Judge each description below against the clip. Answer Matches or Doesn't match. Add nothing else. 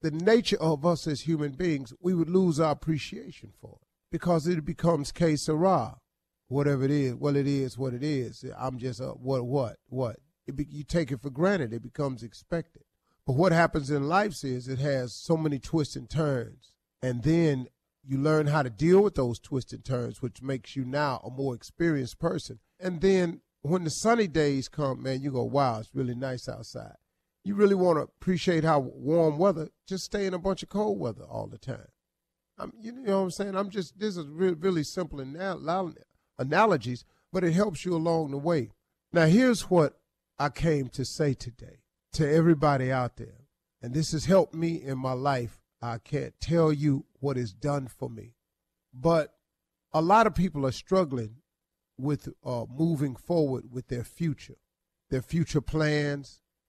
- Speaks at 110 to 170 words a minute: Doesn't match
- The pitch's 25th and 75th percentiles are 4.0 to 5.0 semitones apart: Matches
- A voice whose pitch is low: Doesn't match